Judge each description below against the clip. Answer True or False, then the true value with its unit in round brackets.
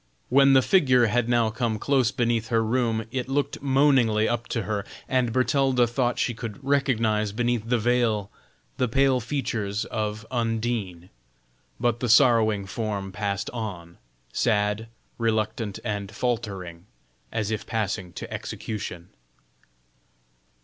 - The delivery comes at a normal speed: False (130 wpm)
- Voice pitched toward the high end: False (115 Hz)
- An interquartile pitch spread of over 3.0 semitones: False (2.6 semitones)